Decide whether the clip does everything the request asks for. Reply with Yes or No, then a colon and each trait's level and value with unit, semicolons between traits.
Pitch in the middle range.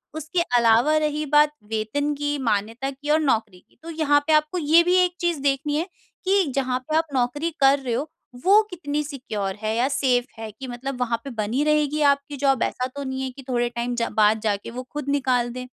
No: very high, 275 Hz